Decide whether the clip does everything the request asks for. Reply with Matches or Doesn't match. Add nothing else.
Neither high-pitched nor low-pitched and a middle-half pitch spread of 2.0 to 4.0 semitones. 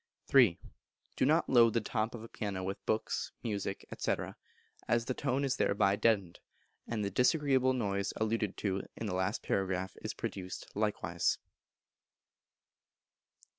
Doesn't match